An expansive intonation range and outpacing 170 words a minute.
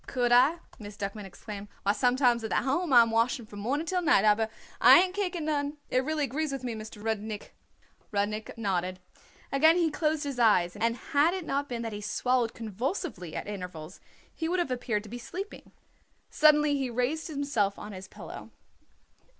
Yes: wide, 6.0 semitones; average, 190 wpm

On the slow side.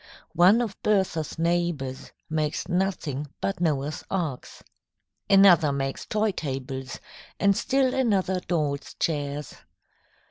Yes: slow, 105 wpm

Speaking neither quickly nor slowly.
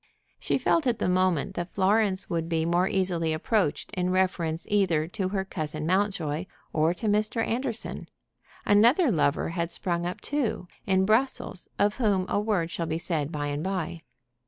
Yes: average, 170 wpm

